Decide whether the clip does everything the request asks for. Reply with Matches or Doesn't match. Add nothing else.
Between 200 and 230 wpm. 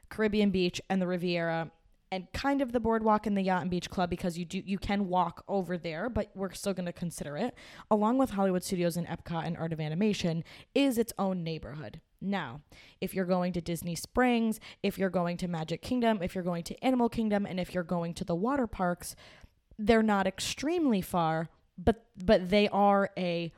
Matches